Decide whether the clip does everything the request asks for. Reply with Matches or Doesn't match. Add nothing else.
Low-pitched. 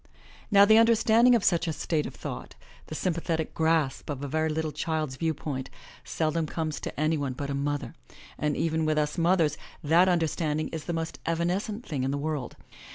Doesn't match